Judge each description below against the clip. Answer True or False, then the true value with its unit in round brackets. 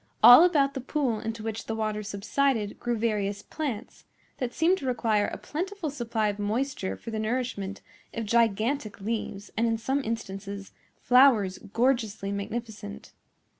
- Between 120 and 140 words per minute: False (150 wpm)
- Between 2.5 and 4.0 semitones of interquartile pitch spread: True (3.7 semitones)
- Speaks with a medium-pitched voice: False (225 Hz)